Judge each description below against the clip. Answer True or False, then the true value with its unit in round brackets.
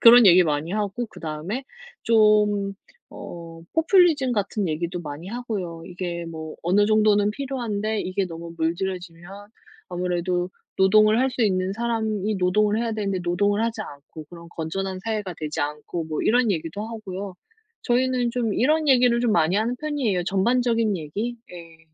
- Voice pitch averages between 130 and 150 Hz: False (200 Hz)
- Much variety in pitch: False (4.7 semitones)